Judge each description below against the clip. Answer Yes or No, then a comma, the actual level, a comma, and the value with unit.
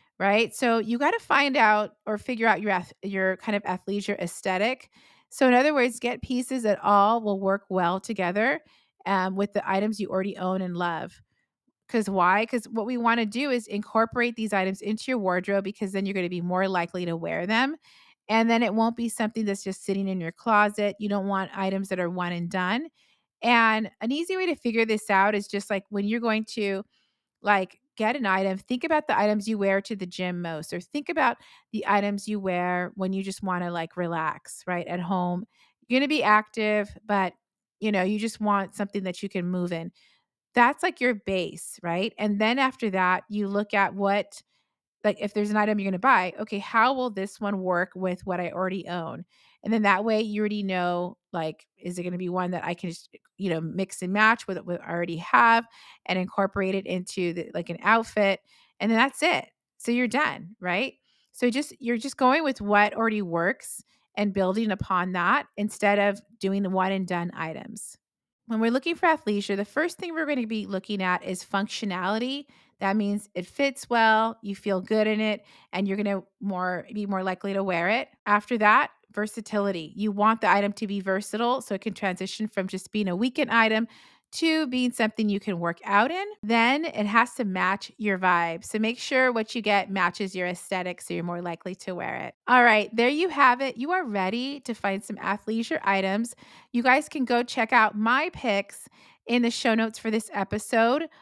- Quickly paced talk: Yes, fast, 215 wpm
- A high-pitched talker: Yes, high, 205 Hz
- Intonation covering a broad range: No, average, 3.4 semitones